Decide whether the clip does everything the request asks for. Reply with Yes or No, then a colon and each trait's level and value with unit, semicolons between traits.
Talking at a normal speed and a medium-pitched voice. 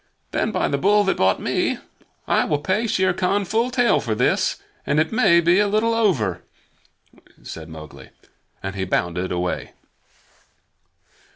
Yes: average, 155 wpm; medium, 170 Hz